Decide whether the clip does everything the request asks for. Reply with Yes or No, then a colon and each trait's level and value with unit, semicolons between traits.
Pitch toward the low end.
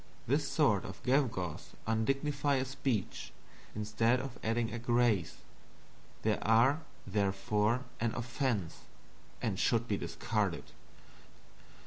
Yes: low, 120 Hz